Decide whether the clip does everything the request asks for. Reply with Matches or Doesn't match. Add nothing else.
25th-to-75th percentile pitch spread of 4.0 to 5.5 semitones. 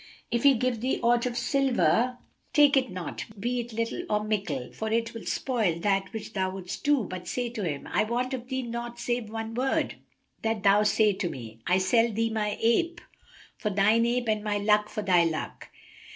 Doesn't match